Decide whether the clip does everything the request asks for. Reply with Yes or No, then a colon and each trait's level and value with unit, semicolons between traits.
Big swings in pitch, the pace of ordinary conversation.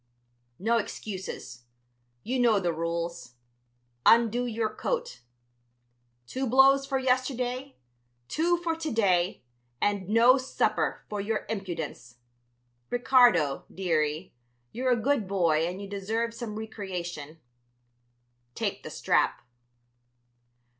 No: wide, 6.3 semitones; slow, 105 wpm